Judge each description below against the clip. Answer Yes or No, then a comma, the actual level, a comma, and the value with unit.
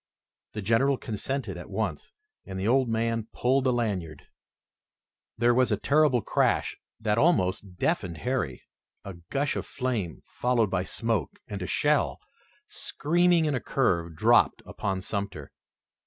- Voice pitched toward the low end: Yes, low, 115 Hz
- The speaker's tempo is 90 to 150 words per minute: Yes, average, 140 wpm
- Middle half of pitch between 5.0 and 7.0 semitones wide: Yes, wide, 5.5 semitones